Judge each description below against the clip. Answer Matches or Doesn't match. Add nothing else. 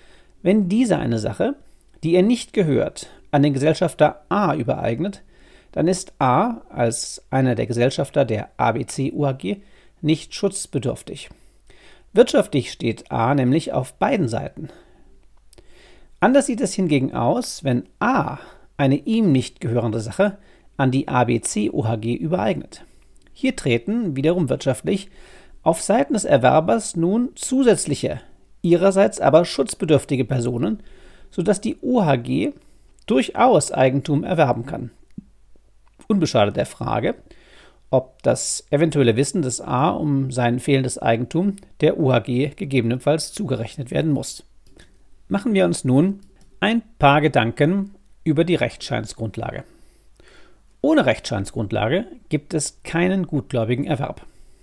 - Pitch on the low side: Doesn't match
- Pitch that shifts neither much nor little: Doesn't match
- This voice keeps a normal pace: Doesn't match